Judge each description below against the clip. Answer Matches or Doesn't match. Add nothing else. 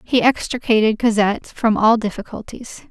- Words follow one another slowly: Matches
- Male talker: Doesn't match